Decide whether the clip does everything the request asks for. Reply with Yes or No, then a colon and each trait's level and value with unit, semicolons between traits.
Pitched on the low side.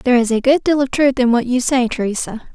No: very high, 250 Hz